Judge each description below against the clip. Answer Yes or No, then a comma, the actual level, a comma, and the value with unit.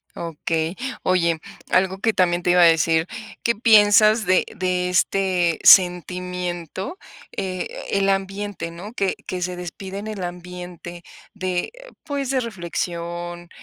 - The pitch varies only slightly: Yes, narrow, 2.1 semitones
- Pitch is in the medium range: Yes, medium, 180 Hz